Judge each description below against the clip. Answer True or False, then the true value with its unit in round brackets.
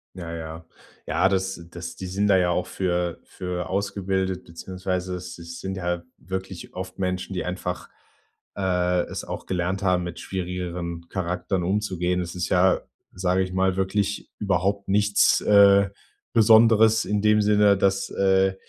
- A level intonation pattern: True (1.6 semitones)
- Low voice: True (95 Hz)